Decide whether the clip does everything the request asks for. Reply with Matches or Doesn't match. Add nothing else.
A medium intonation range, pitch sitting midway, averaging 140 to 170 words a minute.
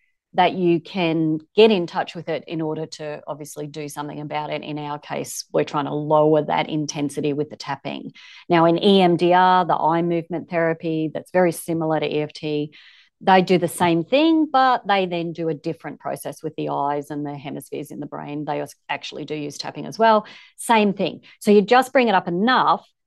Doesn't match